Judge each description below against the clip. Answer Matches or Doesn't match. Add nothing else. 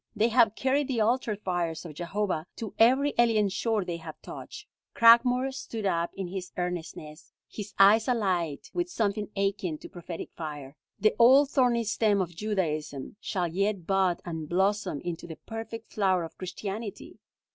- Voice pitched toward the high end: Matches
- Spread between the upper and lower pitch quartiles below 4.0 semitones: Doesn't match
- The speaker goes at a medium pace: Matches